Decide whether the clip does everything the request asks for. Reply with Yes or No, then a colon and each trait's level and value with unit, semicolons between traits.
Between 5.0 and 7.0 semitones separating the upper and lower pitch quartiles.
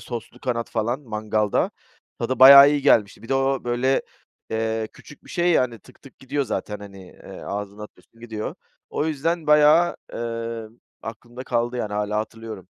No: average, 3.8 semitones